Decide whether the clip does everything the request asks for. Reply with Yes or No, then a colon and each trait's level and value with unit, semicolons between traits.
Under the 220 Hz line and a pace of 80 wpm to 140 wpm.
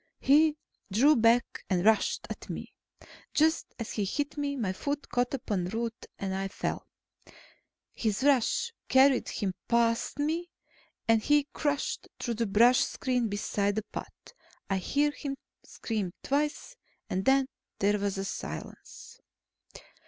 No: high, 235 Hz; slow, 135 wpm